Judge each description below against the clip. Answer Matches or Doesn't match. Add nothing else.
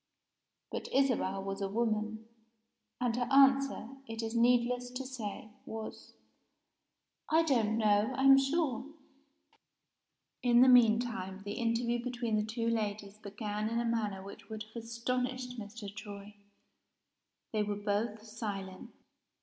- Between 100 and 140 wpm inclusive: Matches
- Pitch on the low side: Doesn't match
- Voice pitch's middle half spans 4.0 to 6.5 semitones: Doesn't match